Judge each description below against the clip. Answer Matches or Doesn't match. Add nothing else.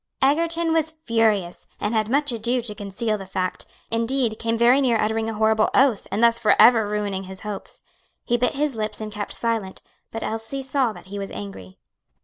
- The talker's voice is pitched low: Doesn't match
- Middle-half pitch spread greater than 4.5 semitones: Doesn't match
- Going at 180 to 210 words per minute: Matches